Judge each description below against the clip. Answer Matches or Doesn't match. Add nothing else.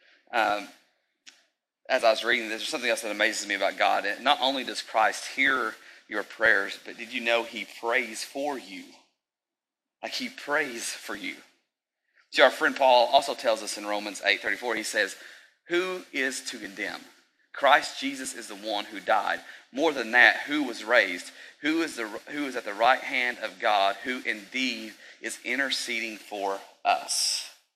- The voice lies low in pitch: Matches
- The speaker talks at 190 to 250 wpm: Doesn't match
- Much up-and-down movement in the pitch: Matches